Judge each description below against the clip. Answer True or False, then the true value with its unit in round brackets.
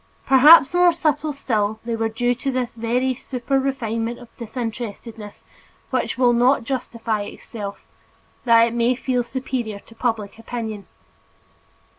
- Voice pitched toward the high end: True (240 Hz)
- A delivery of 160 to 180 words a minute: False (135 wpm)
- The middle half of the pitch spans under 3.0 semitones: True (2.5 semitones)